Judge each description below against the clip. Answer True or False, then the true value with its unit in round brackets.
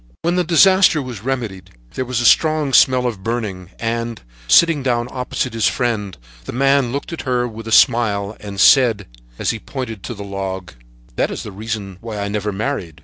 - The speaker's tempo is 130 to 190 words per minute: False (200 wpm)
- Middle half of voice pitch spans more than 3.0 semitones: True (4.2 semitones)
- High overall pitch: False (115 Hz)